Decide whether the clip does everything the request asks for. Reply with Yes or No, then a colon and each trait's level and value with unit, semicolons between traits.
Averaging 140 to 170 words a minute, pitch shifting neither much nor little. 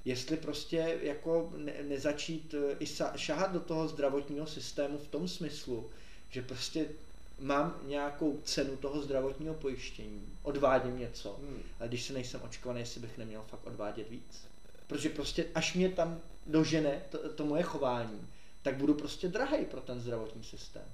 Yes: average, 150 wpm; average, 3.8 semitones